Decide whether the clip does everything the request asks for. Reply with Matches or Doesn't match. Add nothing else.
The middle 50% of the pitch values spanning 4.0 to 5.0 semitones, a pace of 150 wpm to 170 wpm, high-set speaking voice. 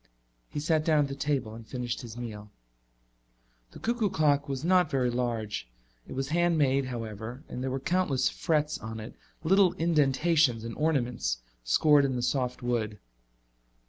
Doesn't match